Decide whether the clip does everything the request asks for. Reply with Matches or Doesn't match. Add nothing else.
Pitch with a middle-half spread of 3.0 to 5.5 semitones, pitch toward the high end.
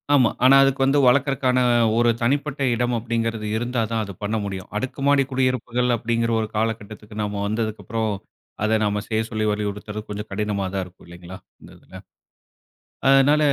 Doesn't match